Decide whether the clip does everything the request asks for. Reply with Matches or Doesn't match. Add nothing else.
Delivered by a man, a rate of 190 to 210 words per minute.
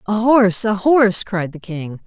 Doesn't match